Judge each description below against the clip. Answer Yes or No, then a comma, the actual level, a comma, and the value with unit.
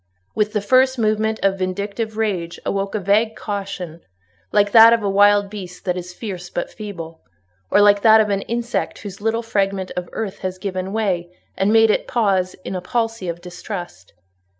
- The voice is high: Yes, high, 200 Hz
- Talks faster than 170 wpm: Yes, average, 180 wpm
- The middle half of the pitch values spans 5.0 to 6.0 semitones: No, average, 3.0 semitones